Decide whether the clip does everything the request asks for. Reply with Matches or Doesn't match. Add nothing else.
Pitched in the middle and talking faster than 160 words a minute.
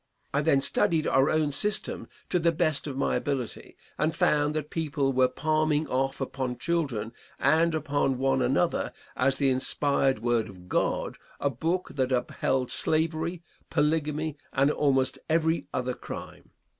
Doesn't match